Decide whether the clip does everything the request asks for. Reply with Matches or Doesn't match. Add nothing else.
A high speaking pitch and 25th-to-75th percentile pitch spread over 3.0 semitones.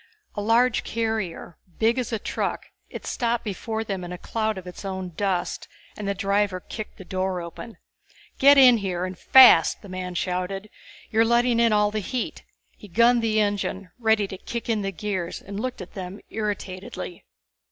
Matches